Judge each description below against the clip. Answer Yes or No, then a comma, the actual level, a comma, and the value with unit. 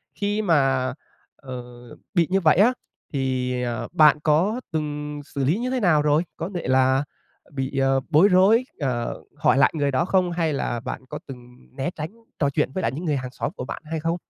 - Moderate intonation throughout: Yes, average, 4.5 semitones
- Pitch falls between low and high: Yes, medium, 150 Hz